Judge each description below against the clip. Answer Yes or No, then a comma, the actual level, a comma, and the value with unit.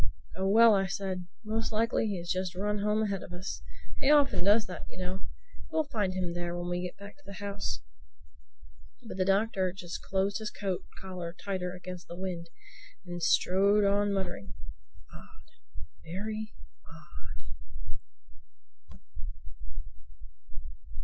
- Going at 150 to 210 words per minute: No, average, 140 wpm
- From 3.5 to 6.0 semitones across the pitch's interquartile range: No, narrow, 2.5 semitones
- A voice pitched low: No, high, 190 Hz